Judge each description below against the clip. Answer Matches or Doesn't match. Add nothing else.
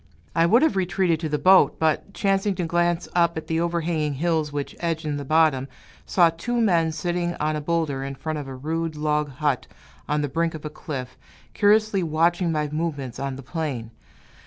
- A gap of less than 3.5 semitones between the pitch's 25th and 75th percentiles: Matches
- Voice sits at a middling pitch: Matches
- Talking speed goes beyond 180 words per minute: Matches